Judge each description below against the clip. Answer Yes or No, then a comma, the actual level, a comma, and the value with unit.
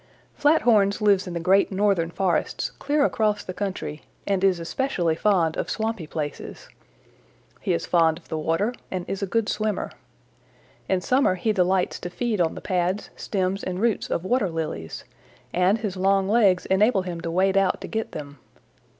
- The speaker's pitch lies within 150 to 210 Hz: Yes, high, 190 Hz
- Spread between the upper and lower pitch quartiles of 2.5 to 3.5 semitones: Yes, average, 3.2 semitones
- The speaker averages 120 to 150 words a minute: No, average, 175 wpm